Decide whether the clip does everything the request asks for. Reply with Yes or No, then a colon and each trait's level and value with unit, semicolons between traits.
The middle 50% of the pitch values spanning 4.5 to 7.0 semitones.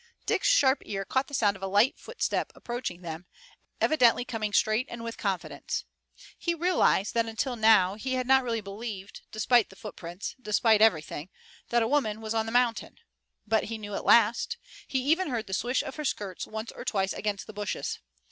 No: average, 3.6 semitones